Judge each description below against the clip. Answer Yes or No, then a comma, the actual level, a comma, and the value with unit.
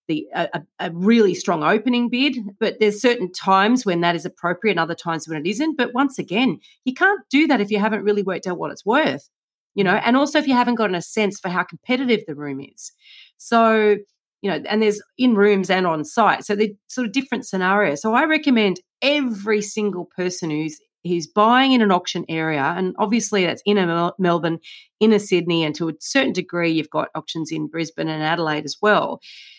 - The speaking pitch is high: Yes, high, 205 Hz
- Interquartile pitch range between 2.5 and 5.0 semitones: No, wide, 5.5 semitones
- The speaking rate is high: Yes, fast, 215 wpm